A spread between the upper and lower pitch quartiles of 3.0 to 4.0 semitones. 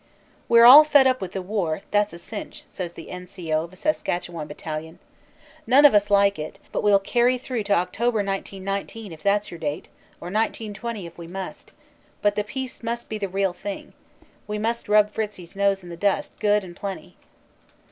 Yes: average, 3.6 semitones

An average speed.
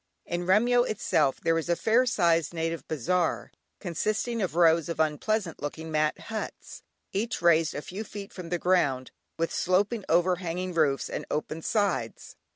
Yes: average, 160 wpm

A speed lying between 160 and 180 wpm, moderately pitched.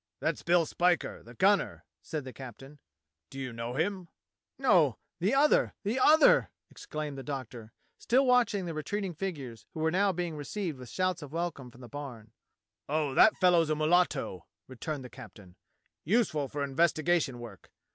Yes: average, 165 wpm; medium, 155 Hz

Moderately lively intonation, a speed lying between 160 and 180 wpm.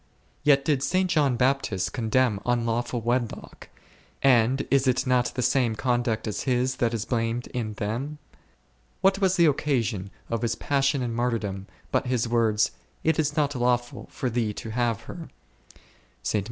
Yes: average, 3.1 semitones; average, 165 wpm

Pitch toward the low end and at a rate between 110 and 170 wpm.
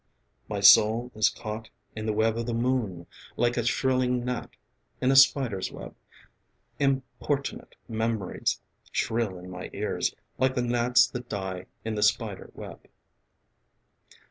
Yes: low, 115 Hz; average, 140 wpm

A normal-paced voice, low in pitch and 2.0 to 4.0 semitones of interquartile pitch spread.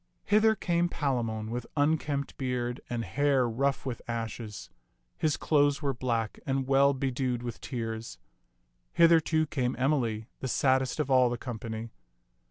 Yes: average, 145 wpm; low, 130 Hz; average, 3.4 semitones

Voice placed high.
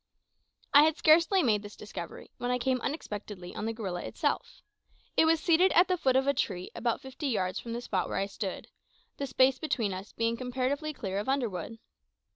Yes: high, 245 Hz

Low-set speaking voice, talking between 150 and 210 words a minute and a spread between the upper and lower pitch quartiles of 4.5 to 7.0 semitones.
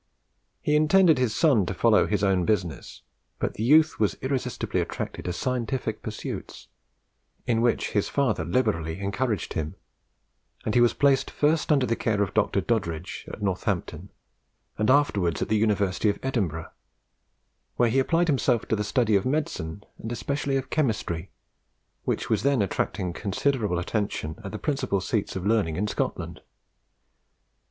Yes: low, 110 Hz; average, 155 wpm; average, 5.2 semitones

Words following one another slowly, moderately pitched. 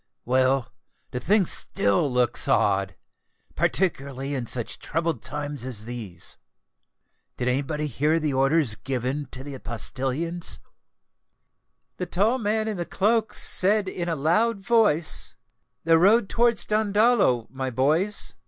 Yes: slow, 120 wpm; medium, 150 Hz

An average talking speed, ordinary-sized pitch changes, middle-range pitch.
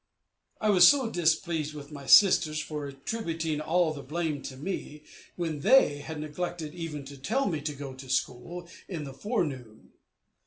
Yes: average, 160 wpm; average, 3.5 semitones; medium, 155 Hz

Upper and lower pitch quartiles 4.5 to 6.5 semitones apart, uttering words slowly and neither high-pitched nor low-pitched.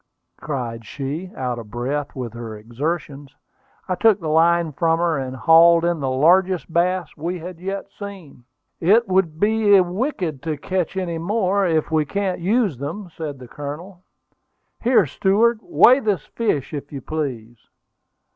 No: average, 5.2 semitones; average, 155 wpm; medium, 165 Hz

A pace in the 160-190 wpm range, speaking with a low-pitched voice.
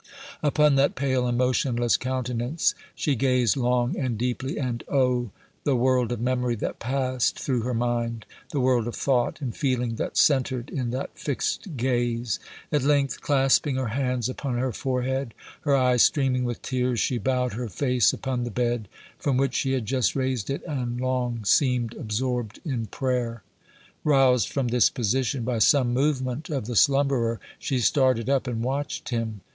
Yes: average, 170 wpm; low, 125 Hz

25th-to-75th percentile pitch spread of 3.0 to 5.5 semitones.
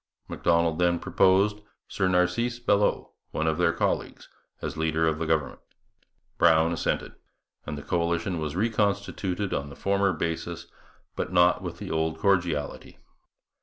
Yes: average, 3.4 semitones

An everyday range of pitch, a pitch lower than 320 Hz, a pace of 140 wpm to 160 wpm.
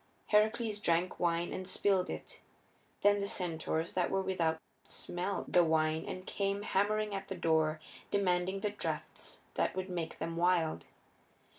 Yes: average, 3.1 semitones; medium, 185 Hz; average, 150 wpm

